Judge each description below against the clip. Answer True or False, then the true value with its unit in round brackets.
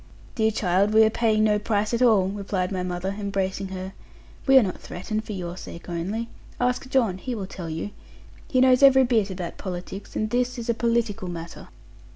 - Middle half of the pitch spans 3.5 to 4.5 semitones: True (3.8 semitones)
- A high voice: True (205 Hz)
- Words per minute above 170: True (195 wpm)